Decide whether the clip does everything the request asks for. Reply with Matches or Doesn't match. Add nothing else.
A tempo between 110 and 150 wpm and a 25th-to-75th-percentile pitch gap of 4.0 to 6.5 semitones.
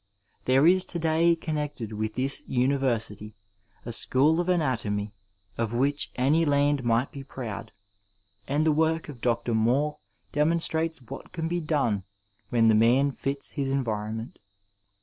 Matches